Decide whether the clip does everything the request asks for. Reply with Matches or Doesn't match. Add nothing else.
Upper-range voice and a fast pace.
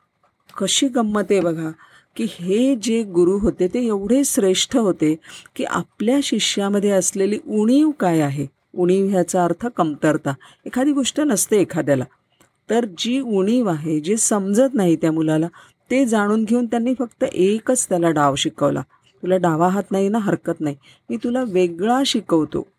Matches